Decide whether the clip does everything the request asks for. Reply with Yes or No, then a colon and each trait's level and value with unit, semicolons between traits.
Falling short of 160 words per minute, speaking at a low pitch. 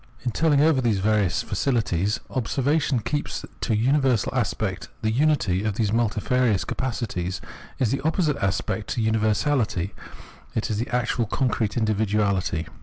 Yes: average, 140 wpm; low, 115 Hz